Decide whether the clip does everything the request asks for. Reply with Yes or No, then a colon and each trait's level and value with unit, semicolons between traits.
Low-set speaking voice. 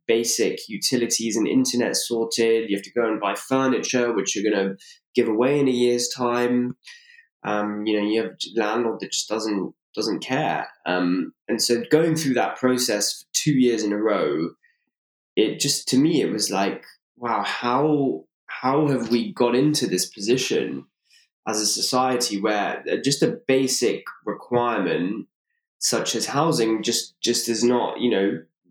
Yes: low, 120 Hz